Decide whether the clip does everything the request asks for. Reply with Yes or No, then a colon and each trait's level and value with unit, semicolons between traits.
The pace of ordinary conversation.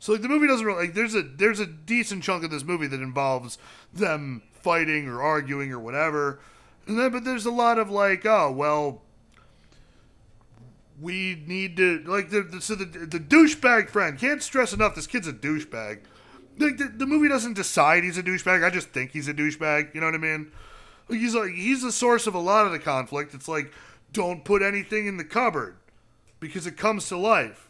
No: fast, 210 wpm